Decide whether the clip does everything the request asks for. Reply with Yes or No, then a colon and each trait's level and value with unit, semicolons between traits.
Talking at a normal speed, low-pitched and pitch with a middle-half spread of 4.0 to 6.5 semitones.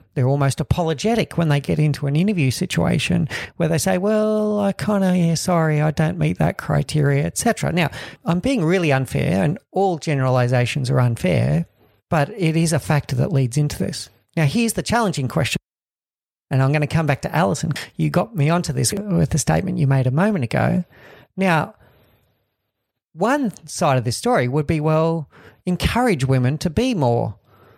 No: average, 180 wpm; medium, 155 Hz; average, 4.9 semitones